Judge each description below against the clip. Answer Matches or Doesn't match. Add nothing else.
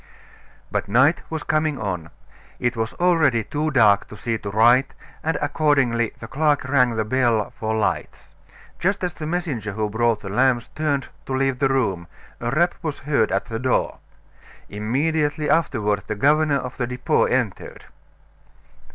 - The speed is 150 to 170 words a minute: Matches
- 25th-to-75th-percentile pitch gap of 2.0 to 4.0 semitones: Doesn't match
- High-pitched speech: Doesn't match